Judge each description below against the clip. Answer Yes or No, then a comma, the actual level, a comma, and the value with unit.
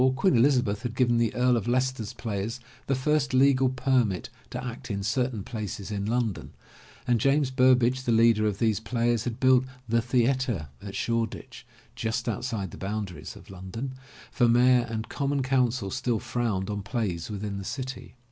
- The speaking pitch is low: Yes, low, 120 Hz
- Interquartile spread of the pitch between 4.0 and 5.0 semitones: No, average, 3.2 semitones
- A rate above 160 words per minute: Yes, average, 170 wpm